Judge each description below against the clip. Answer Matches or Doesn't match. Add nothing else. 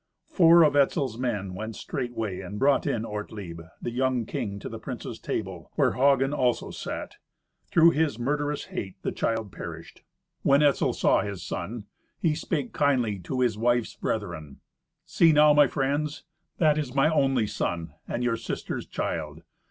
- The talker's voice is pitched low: Matches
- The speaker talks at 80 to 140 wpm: Doesn't match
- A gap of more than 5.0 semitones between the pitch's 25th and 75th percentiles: Matches